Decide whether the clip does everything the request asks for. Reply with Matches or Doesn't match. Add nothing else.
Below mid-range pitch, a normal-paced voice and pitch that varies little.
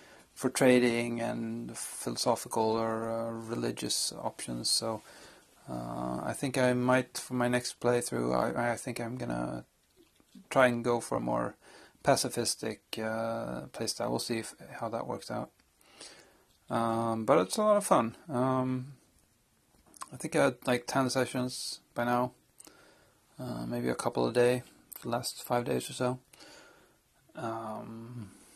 Matches